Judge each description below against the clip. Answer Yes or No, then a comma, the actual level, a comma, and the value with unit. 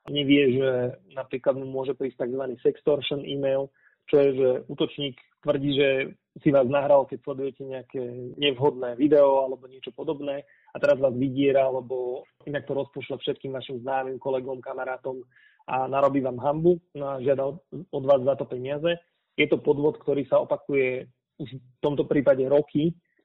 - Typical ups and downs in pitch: No, narrow, 1.7 semitones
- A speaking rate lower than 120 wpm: No, average, 155 wpm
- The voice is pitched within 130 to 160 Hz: Yes, medium, 140 Hz